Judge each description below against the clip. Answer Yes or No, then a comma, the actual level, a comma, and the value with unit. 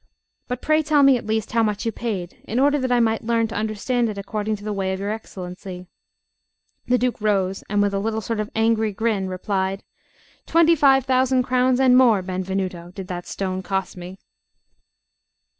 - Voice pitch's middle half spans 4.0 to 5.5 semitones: Yes, average, 4.3 semitones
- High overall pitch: Yes, high, 215 Hz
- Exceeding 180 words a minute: Yes, average, 190 wpm